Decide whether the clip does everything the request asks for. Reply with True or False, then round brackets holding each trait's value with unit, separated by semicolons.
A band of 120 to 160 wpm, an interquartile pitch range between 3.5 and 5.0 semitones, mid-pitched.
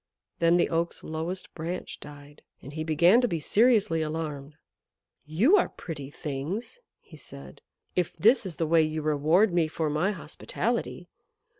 False (155 wpm; 3.1 semitones; 165 Hz)